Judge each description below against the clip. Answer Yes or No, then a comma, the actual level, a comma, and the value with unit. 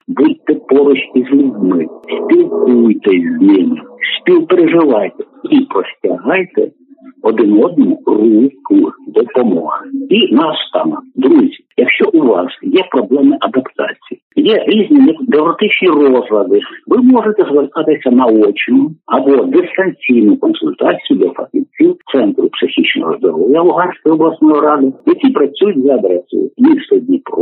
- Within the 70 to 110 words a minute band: Yes, slow, 105 wpm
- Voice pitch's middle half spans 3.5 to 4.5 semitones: No, wide, 5.5 semitones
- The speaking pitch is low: No, very high, 300 Hz